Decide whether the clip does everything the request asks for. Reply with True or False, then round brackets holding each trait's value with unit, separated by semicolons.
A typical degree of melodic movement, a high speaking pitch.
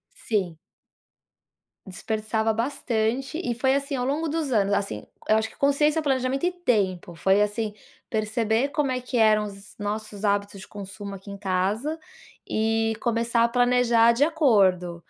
True (4.1 semitones; 225 Hz)